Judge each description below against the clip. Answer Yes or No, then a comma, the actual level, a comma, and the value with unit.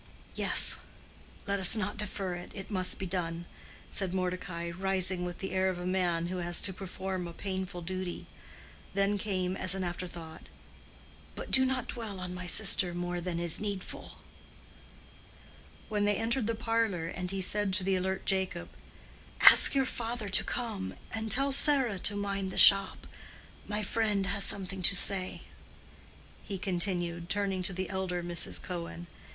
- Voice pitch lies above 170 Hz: Yes, high, 190 Hz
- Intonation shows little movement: Yes, narrow, 2.3 semitones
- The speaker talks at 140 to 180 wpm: Yes, average, 160 wpm